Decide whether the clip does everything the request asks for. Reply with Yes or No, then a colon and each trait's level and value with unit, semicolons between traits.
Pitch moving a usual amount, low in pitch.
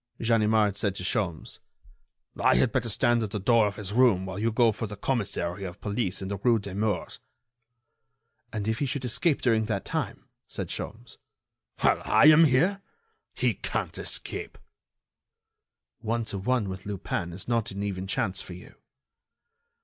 Yes: average, 3.2 semitones; low, 105 Hz